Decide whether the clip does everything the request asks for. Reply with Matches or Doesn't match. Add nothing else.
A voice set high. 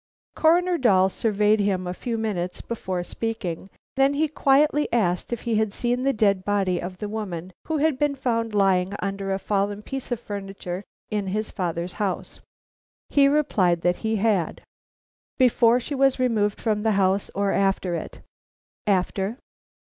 Matches